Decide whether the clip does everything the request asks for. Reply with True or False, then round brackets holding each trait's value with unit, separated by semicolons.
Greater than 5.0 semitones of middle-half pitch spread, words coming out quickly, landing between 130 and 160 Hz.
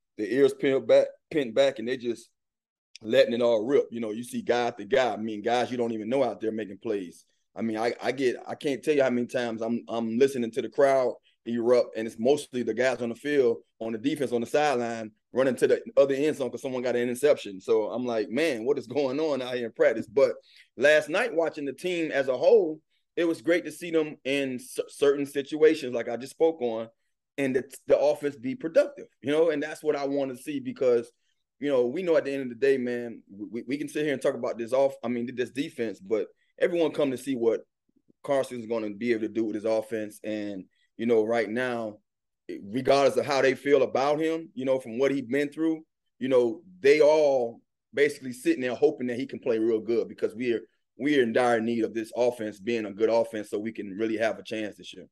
True (5.4 semitones; 245 wpm; 135 Hz)